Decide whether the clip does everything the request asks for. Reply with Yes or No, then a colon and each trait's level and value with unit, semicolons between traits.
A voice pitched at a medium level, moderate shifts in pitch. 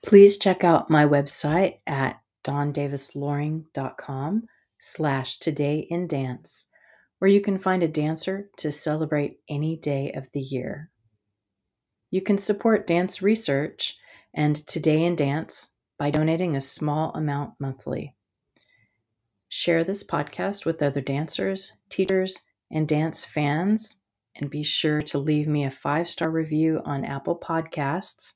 Yes: medium, 155 Hz; average, 3.3 semitones